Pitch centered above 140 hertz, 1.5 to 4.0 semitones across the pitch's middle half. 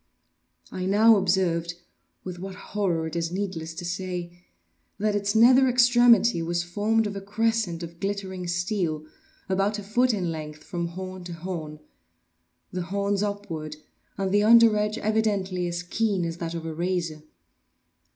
Yes: medium, 185 Hz; average, 3.4 semitones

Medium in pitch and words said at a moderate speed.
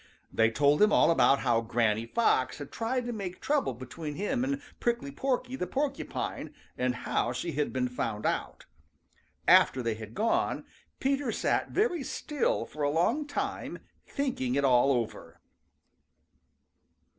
Yes: medium, 155 Hz; average, 150 wpm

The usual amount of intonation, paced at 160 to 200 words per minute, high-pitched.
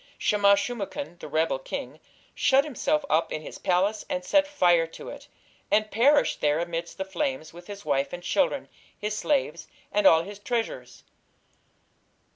No: wide, 5.8 semitones; average, 165 wpm; high, 195 Hz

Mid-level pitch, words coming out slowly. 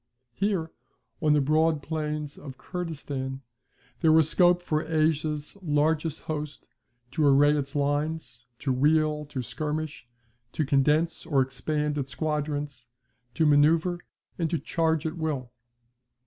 Yes: medium, 150 Hz; slow, 130 wpm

